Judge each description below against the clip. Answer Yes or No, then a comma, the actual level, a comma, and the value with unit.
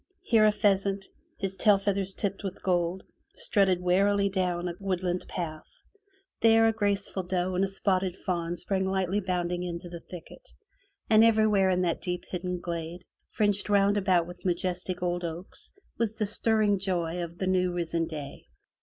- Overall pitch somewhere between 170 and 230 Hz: Yes, medium, 185 Hz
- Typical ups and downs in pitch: No, narrow, 2.2 semitones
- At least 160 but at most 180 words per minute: Yes, average, 165 wpm